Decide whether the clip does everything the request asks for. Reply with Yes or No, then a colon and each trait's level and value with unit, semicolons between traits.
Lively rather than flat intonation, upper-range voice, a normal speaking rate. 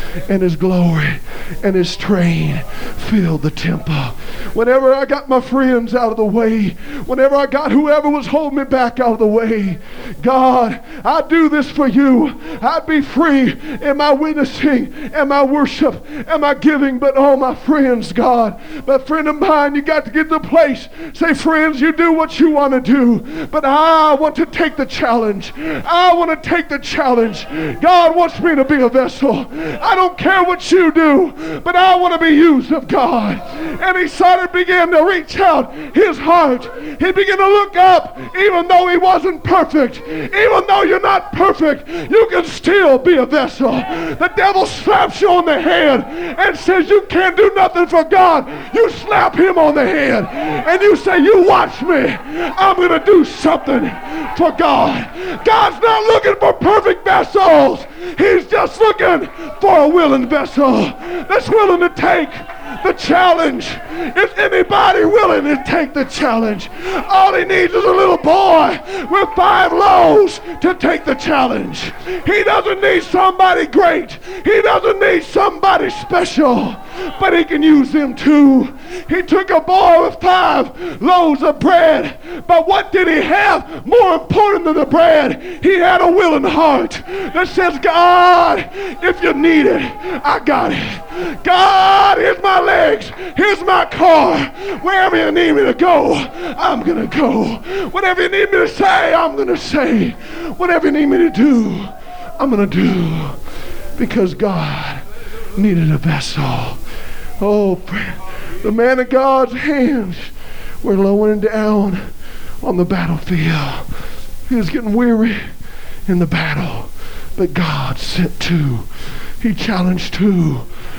Yes: wide, 6.0 semitones; very high, 315 Hz; average, 160 wpm